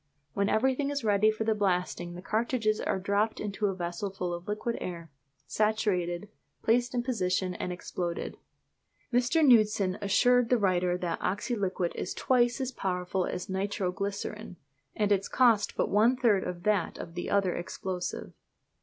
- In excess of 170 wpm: No, average, 160 wpm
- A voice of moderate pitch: No, high, 200 Hz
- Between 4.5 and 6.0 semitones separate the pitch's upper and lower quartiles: No, average, 3.7 semitones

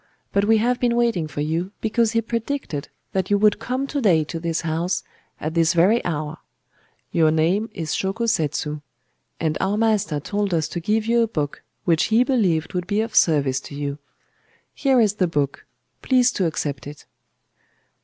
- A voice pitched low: No, medium, 185 Hz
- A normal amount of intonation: No, wide, 6.1 semitones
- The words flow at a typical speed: Yes, average, 180 wpm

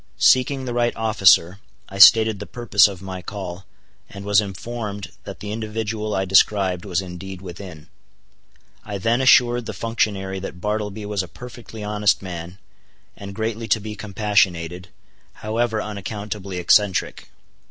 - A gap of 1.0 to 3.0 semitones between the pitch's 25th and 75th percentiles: Yes, narrow, 2.6 semitones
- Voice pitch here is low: Yes, low, 105 Hz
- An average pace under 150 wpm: Yes, average, 140 wpm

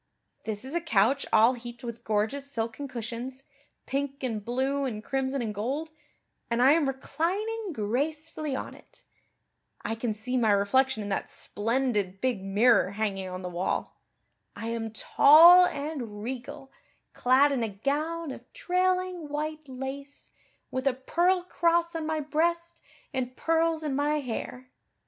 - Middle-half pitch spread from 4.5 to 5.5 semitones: Yes, average, 5.2 semitones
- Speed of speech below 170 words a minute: Yes, average, 150 wpm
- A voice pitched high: Yes, very high, 265 Hz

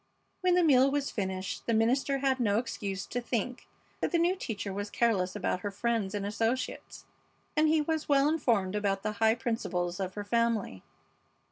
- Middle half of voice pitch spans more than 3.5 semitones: Yes, average, 5.1 semitones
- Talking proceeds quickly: No, average, 180 wpm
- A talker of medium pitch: No, high, 225 Hz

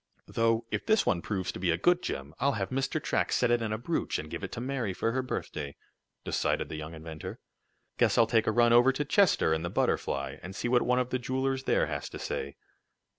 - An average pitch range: No, wide, 6.8 semitones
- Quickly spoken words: Yes, fast, 240 wpm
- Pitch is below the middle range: Yes, low, 115 Hz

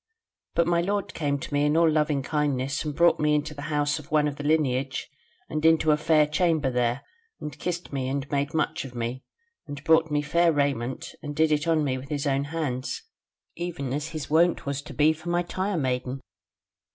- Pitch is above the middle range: No, medium, 150 Hz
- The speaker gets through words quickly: Yes, fast, 215 wpm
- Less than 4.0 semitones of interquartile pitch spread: Yes, narrow, 2.4 semitones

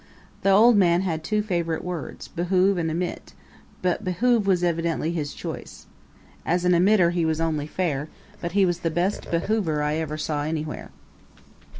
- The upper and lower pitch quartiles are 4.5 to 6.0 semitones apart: No, average, 2.8 semitones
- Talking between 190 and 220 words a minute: No, average, 170 wpm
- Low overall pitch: No, medium, 170 Hz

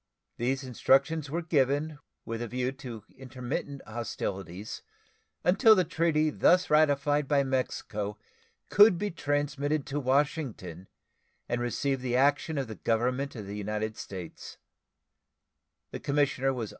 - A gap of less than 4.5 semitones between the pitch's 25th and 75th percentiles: Yes, average, 4.0 semitones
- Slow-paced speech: Yes, slow, 120 wpm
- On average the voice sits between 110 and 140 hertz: Yes, low, 135 Hz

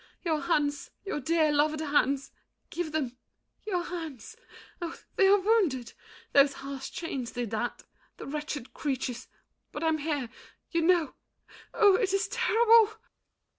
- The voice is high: Yes, very high, 310 Hz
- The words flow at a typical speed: No, slow, 130 wpm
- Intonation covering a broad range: No, average, 4.6 semitones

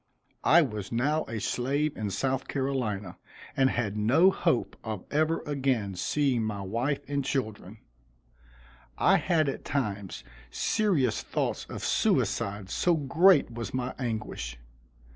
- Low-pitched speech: Yes, low, 125 Hz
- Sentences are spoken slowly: Yes, slow, 130 wpm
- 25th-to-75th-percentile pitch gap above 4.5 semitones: Yes, average, 5.2 semitones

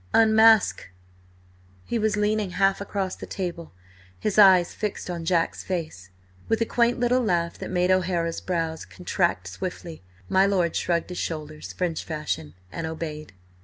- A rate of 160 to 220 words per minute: No, average, 150 wpm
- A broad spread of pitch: No, average, 3.5 semitones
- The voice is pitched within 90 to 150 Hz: No, medium, 180 Hz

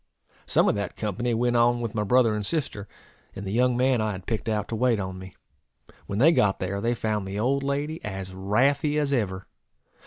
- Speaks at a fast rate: Yes, fast, 215 wpm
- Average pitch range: Yes, average, 4.1 semitones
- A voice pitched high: No, low, 110 Hz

